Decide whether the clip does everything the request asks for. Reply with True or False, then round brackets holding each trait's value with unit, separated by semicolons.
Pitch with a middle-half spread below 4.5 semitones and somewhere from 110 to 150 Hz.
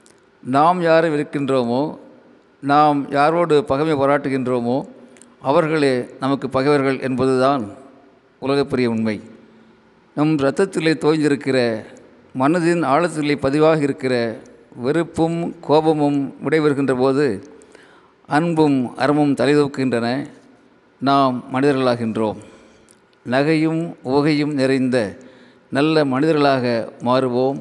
True (2.5 semitones; 140 Hz)